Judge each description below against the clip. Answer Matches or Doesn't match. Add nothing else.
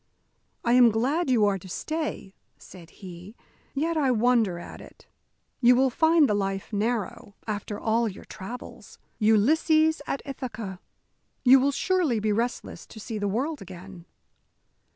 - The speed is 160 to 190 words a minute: Doesn't match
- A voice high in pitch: Matches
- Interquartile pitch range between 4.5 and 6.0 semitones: Matches